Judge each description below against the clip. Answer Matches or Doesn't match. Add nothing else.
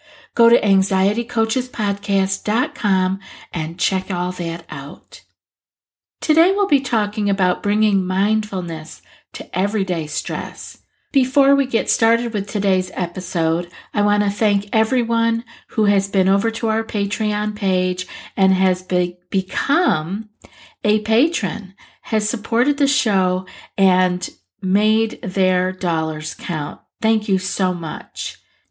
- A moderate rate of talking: Doesn't match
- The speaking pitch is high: Matches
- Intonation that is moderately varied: Matches